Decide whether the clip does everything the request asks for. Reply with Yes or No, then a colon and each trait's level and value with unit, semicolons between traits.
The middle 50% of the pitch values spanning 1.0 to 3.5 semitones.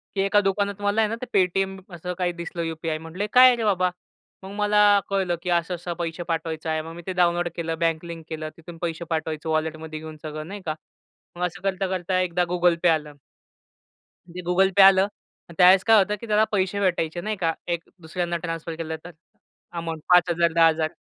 Yes: average, 2.9 semitones